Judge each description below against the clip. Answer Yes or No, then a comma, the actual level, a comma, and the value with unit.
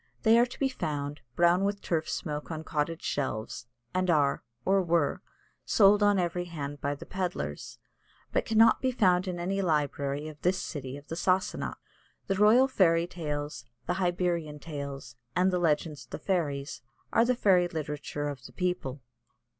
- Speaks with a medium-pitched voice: Yes, medium, 170 Hz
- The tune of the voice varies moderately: Yes, average, 4.2 semitones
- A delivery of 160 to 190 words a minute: Yes, average, 170 wpm